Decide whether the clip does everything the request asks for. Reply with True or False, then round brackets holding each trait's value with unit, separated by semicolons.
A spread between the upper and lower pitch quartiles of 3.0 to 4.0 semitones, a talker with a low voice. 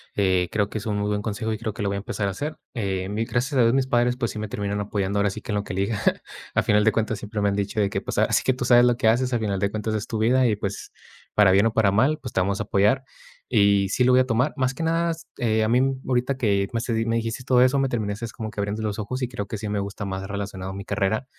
True (3.3 semitones; 110 Hz)